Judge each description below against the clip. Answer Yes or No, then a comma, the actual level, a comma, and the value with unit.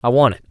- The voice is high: No, low, 120 Hz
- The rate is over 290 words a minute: Yes, fast, 360 wpm